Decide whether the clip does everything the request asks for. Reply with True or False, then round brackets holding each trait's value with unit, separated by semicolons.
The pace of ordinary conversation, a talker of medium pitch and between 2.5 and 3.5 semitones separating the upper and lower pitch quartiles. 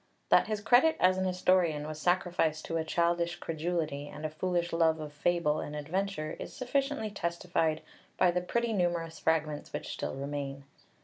True (175 wpm; 170 Hz; 3.0 semitones)